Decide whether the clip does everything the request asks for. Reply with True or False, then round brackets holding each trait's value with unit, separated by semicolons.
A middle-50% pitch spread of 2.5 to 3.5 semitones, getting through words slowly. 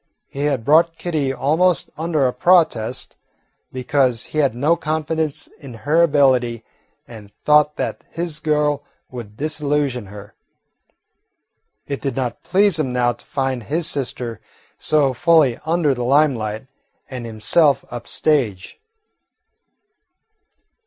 False (4.1 semitones; 125 wpm)